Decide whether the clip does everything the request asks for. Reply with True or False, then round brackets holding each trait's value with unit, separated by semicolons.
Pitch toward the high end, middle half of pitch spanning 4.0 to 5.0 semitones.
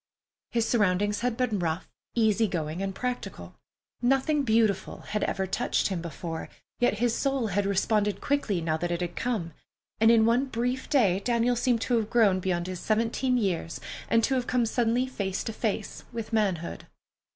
True (220 Hz; 4.3 semitones)